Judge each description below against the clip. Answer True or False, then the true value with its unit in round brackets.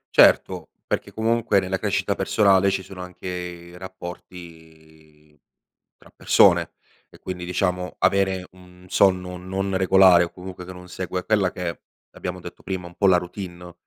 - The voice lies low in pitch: True (90 Hz)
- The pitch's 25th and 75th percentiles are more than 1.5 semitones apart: False (1.2 semitones)